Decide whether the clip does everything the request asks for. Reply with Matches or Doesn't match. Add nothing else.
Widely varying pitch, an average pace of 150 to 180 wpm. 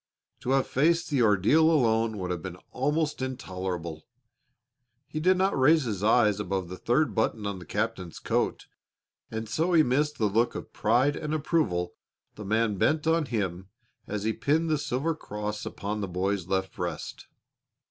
Matches